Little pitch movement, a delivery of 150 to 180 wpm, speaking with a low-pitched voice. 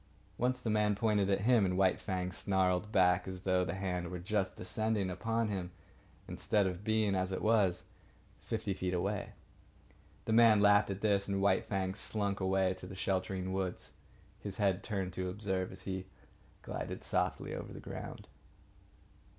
Yes: narrow, 2.1 semitones; average, 170 wpm; very low, 95 Hz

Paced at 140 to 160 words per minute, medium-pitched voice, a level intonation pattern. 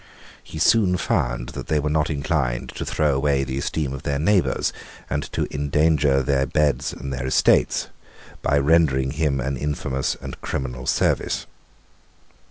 No: average, 155 wpm; very low, 70 Hz; narrow, 2.3 semitones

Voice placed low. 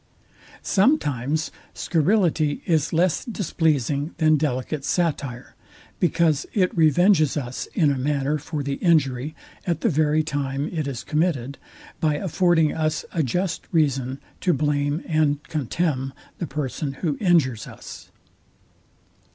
No: medium, 155 Hz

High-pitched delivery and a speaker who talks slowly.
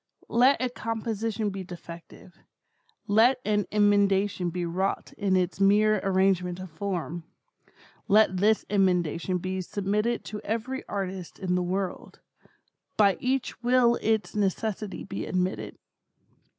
Yes: high, 200 Hz; slow, 125 wpm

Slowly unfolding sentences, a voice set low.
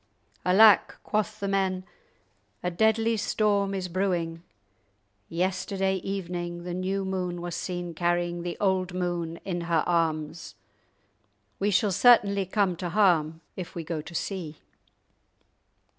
No: slow, 130 wpm; medium, 180 Hz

